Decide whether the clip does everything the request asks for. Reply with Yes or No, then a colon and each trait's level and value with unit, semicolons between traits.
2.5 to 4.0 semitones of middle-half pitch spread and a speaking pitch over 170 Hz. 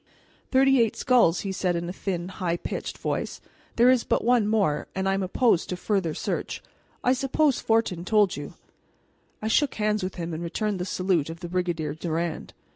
No: average, 4.5 semitones; high, 190 Hz